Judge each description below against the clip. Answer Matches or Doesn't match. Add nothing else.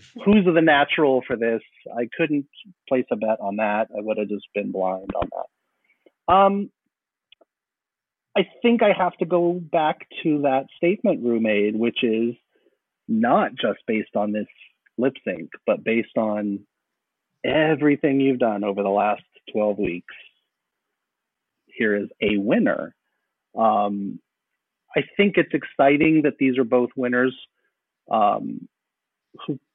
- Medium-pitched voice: Doesn't match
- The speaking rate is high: Doesn't match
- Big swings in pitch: Matches